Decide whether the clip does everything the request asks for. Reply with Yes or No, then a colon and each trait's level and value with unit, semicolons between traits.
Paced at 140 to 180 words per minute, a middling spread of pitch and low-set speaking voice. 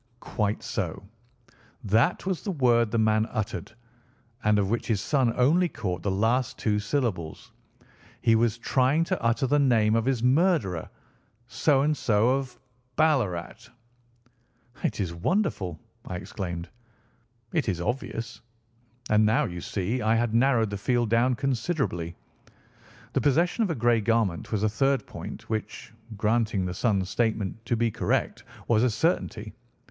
Yes: average, 150 wpm; average, 3.8 semitones; low, 115 Hz